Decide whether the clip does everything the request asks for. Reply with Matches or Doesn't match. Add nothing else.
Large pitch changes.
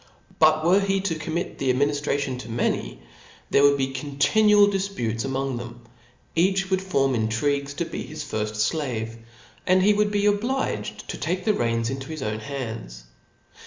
Matches